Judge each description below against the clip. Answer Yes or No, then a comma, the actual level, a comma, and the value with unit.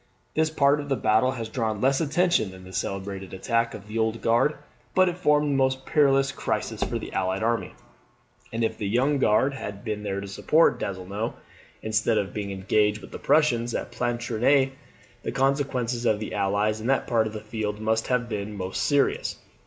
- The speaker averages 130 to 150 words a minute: No, average, 195 wpm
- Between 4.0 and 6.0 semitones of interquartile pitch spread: Yes, average, 4.4 semitones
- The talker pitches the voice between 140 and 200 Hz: No, low, 115 Hz